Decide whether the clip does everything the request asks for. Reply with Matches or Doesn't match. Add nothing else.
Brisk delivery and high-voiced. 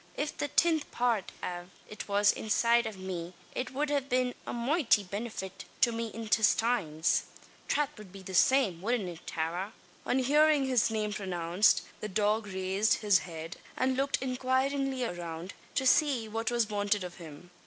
Doesn't match